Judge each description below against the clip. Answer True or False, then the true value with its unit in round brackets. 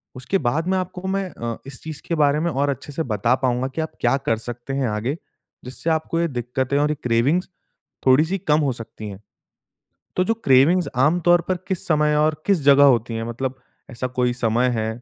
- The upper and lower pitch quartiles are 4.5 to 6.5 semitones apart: True (4.9 semitones)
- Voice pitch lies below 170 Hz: True (140 Hz)